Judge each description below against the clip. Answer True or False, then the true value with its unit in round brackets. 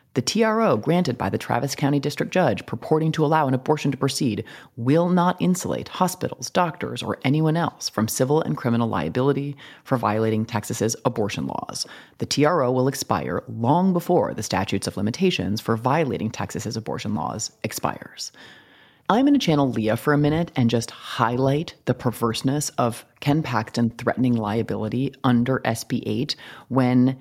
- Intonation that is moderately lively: True (4.7 semitones)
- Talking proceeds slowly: False (160 wpm)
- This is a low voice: True (130 Hz)